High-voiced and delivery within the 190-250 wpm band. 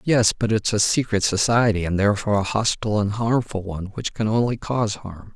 No: low, 105 Hz; average, 200 wpm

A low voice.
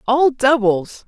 No: high, 245 Hz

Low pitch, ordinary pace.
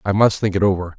No: low, 100 Hz; fast, 305 wpm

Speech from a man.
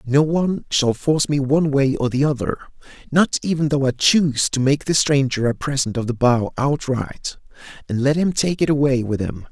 Yes: male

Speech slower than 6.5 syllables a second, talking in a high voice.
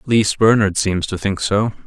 No: 4.7 syllables/s; low, 100 Hz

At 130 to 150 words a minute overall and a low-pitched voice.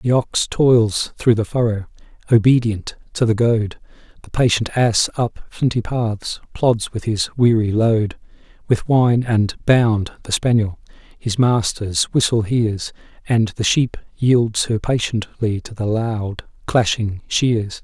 Yes: average, 140 wpm; low, 110 Hz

